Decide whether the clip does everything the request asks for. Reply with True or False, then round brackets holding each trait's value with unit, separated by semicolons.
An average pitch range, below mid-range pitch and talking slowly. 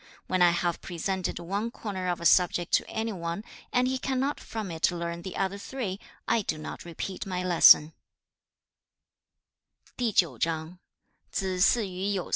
False (3.7 semitones; 185 Hz; 130 wpm)